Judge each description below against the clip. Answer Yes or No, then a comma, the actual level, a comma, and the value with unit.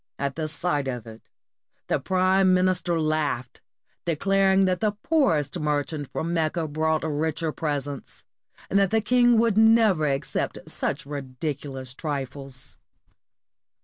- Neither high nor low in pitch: Yes, medium, 155 Hz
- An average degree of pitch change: Yes, average, 4.6 semitones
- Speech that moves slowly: Yes, slow, 120 wpm